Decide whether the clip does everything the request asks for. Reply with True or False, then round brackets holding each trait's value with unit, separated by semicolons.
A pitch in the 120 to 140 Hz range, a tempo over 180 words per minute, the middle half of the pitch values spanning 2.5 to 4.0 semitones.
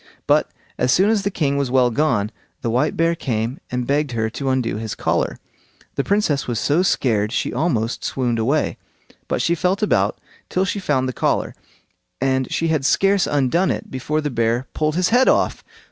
False (135 Hz; 190 wpm; 5.4 semitones)